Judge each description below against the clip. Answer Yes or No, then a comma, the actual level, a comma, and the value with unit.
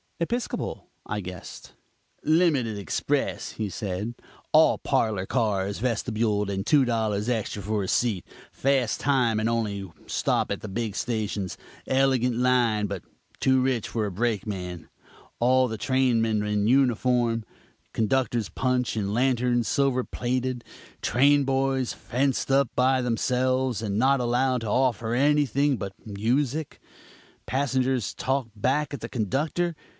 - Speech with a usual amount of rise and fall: Yes, average, 3.6 semitones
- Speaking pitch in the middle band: No, low, 120 Hz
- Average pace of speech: No, slow, 130 wpm